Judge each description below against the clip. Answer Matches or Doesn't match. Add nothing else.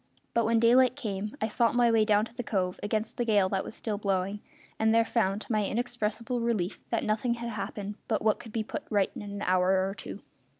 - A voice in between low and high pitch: Doesn't match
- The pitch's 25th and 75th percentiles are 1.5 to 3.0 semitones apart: Matches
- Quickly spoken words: Matches